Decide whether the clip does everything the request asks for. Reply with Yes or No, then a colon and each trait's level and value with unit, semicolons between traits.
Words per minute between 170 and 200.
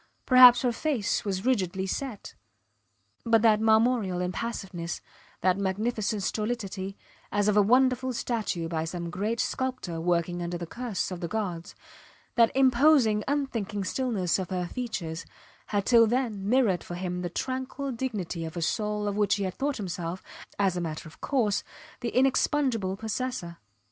No: average, 155 wpm